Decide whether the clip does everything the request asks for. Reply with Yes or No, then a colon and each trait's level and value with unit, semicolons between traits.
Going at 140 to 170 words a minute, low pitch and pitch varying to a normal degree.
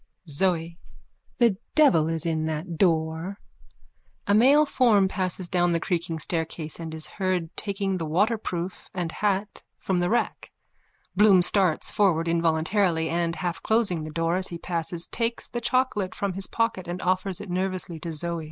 No: average, 160 wpm; medium, 180 Hz; average, 3.1 semitones